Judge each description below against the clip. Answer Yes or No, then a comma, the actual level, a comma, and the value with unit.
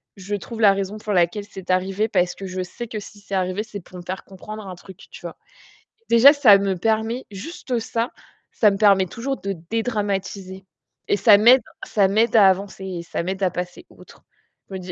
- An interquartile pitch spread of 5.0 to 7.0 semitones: No, narrow, 2.6 semitones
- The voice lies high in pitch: Yes, high, 200 Hz